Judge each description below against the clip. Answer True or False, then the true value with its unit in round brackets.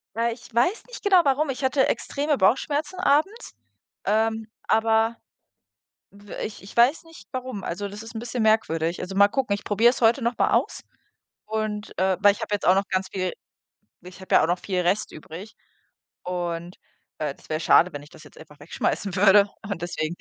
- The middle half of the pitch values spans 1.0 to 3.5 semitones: False (4.6 semitones)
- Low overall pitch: False (210 Hz)